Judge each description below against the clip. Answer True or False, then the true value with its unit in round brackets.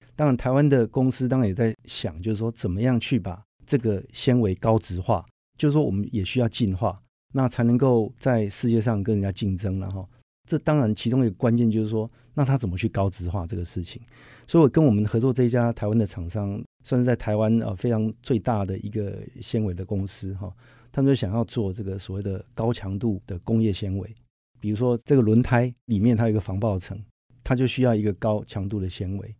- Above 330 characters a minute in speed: False (325 characters per minute)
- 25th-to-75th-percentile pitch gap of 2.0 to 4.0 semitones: True (3.5 semitones)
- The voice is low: True (115 Hz)